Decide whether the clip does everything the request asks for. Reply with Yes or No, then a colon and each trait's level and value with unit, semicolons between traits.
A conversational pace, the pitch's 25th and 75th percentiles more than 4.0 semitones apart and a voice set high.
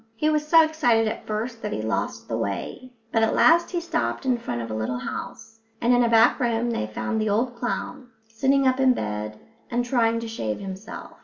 No: fast, 220 wpm; average, 4.9 semitones; high, 230 Hz